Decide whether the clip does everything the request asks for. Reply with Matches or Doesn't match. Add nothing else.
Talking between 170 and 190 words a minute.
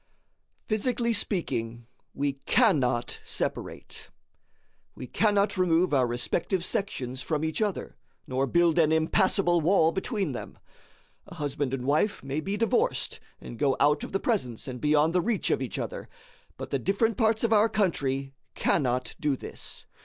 Doesn't match